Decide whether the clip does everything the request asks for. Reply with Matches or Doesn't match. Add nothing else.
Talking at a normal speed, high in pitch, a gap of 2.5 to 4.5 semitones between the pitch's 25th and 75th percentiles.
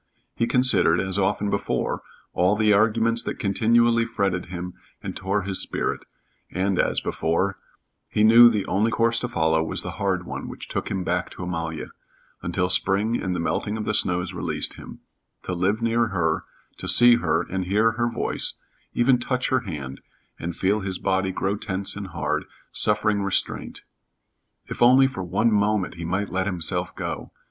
Doesn't match